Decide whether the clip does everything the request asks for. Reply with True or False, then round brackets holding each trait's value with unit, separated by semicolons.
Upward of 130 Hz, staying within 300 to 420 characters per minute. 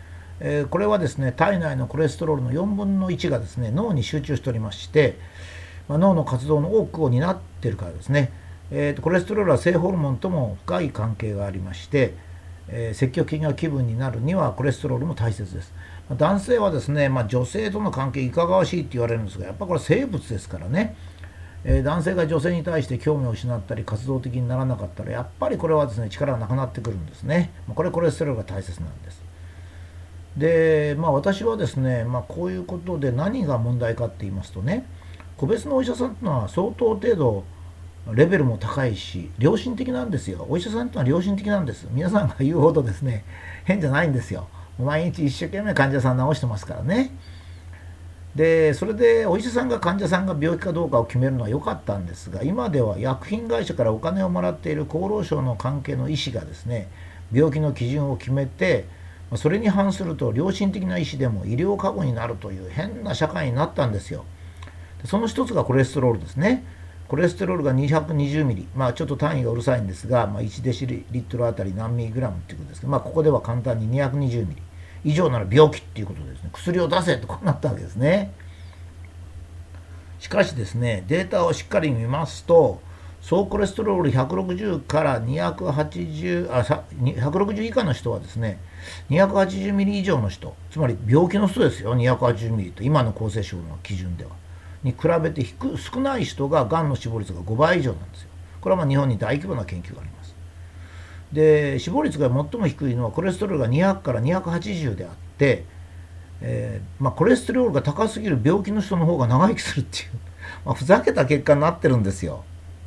False (125 Hz; 400 characters per minute)